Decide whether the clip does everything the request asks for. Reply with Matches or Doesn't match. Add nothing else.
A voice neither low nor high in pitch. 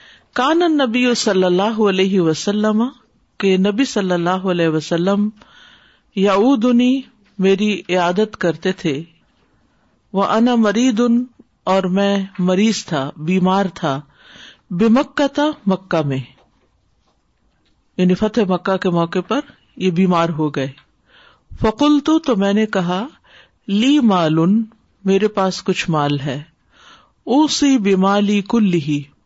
Doesn't match